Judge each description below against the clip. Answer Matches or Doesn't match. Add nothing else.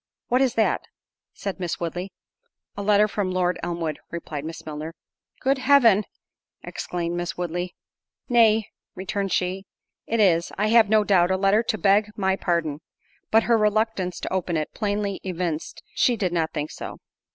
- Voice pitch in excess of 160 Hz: Matches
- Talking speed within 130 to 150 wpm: Doesn't match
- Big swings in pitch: Doesn't match